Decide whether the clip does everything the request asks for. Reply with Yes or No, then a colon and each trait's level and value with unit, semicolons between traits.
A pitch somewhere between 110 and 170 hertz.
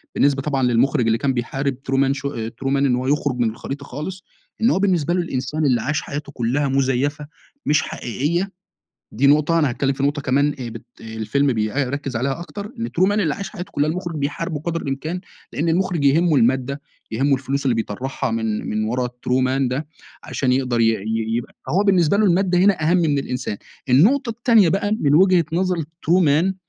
Yes: medium, 140 Hz